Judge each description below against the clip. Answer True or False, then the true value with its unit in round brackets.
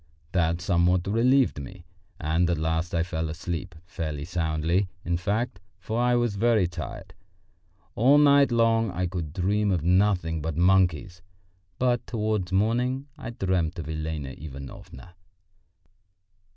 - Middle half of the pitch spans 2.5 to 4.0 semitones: False (5.1 semitones)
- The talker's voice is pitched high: False (90 Hz)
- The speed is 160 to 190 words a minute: False (135 wpm)